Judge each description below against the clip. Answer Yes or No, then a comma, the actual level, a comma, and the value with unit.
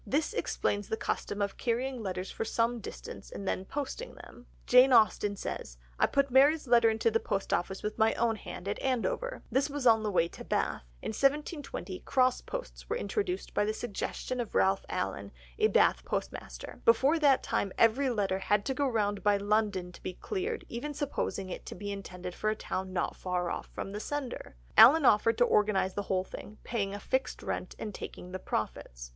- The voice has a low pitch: No, high, 220 Hz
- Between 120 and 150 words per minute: No, average, 200 wpm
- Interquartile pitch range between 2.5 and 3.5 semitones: No, average, 5.3 semitones